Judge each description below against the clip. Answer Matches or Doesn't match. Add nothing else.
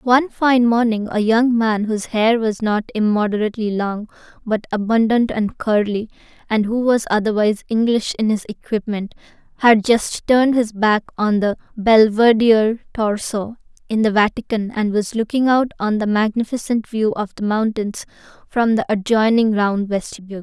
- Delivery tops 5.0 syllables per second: Doesn't match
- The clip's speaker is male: Doesn't match